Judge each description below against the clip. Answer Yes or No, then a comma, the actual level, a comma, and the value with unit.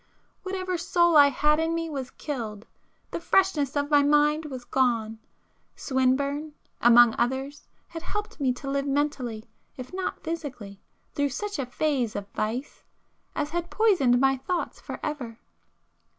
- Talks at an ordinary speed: Yes, average, 145 wpm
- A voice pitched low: No, very high, 285 Hz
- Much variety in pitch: No, average, 4.2 semitones